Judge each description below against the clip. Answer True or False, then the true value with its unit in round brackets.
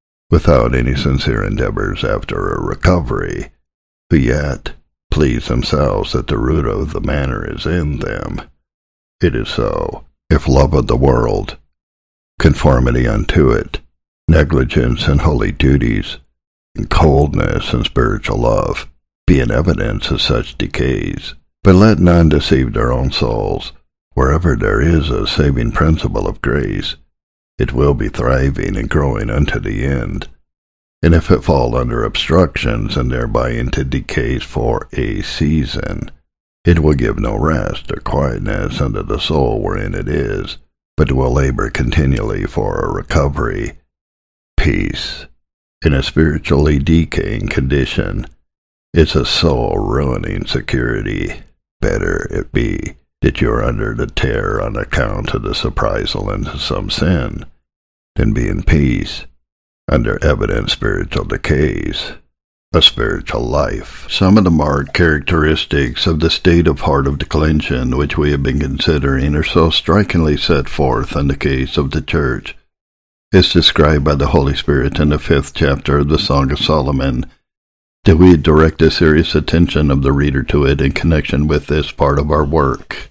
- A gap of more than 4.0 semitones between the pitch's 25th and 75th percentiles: False (2.8 semitones)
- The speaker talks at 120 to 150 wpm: True (145 wpm)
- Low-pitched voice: True (75 Hz)